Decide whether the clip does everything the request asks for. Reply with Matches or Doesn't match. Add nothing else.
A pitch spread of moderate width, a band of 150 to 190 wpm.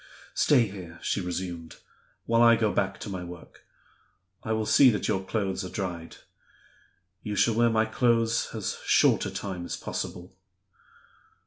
Matches